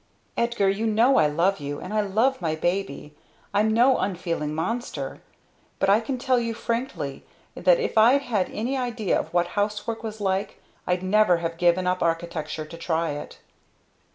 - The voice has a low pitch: No, high, 195 Hz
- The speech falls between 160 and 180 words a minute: Yes, average, 175 wpm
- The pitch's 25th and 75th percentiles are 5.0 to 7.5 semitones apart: Yes, average, 5.3 semitones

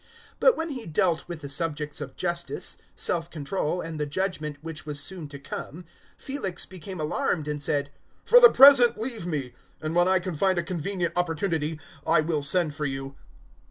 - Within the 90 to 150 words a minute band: No, average, 190 wpm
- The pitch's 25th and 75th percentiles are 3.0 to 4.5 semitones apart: Yes, average, 3.8 semitones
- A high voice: No, medium, 165 Hz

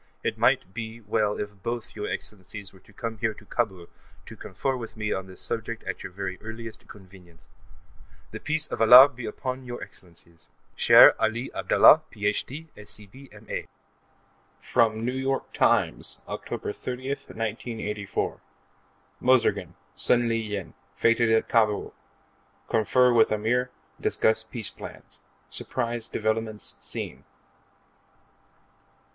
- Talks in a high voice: No, low, 110 Hz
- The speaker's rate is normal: No, slow, 130 wpm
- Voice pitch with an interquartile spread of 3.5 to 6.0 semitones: No, narrow, 2.6 semitones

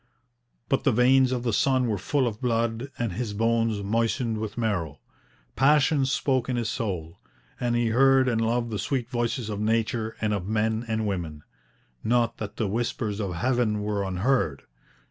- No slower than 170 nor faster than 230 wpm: Yes, average, 175 wpm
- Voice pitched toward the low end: Yes, low, 115 Hz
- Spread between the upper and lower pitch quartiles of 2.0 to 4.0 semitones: Yes, average, 2.7 semitones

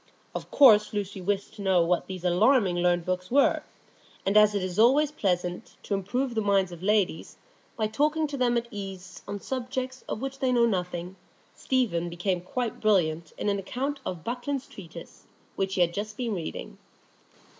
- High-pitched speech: Yes, high, 200 Hz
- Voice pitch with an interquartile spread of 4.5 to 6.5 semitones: Yes, average, 5.3 semitones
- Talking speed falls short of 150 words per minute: No, average, 180 wpm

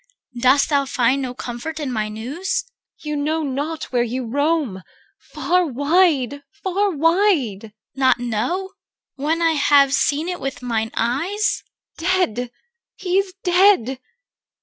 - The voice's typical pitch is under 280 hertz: No, very high, 285 Hz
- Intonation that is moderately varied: No, wide, 5.8 semitones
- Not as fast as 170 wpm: Yes, average, 145 wpm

